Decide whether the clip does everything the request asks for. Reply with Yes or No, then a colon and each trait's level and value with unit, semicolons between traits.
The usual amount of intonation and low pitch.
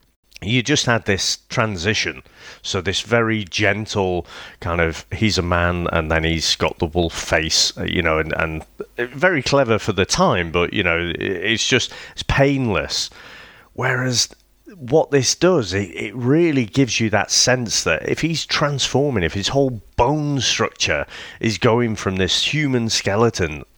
No: wide, 6.7 semitones; low, 110 Hz